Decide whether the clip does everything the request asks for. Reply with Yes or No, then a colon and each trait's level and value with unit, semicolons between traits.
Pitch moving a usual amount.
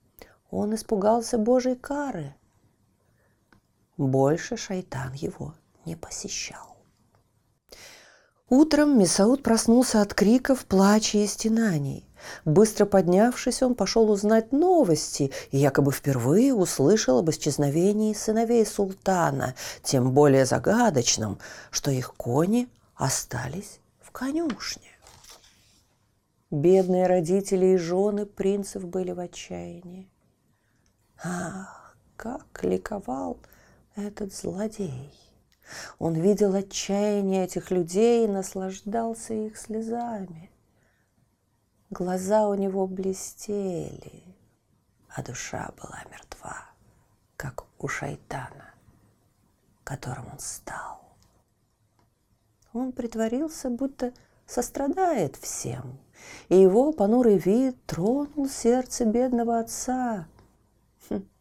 No: wide, 8.7 semitones